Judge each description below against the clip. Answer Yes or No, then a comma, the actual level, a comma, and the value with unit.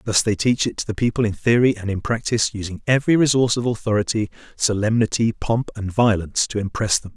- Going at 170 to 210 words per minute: Yes, average, 200 wpm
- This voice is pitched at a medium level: No, low, 110 Hz